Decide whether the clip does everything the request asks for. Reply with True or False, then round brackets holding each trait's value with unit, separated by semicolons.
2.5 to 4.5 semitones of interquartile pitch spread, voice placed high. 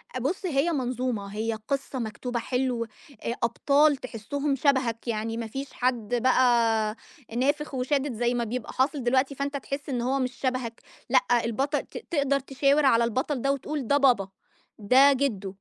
True (3.1 semitones; 255 Hz)